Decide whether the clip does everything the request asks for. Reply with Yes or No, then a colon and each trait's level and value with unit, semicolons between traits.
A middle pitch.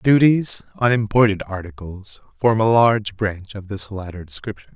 No: low, 105 Hz